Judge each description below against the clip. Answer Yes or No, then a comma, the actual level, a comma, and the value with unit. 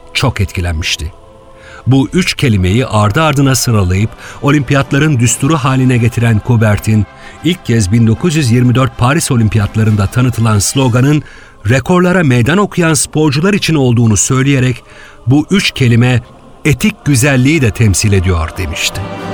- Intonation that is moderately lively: Yes, average, 5.0 semitones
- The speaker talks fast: No, average, 110 wpm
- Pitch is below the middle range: Yes, low, 125 Hz